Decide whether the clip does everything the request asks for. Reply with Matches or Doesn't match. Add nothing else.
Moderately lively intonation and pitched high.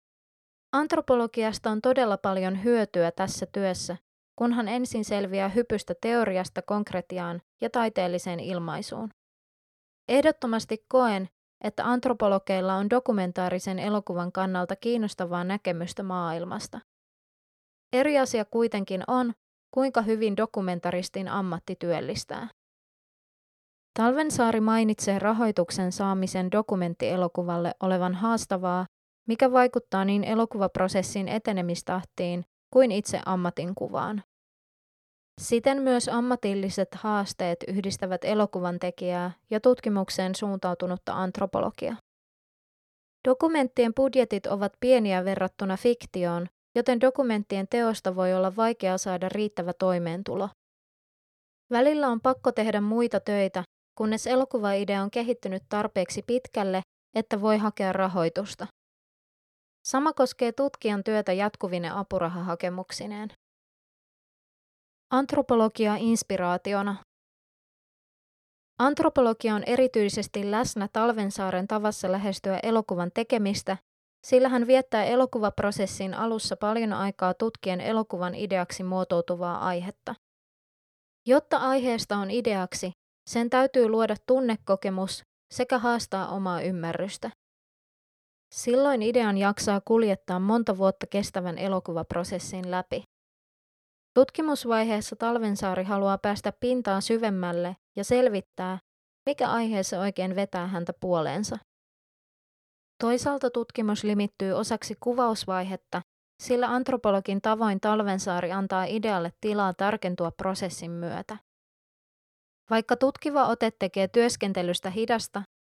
Matches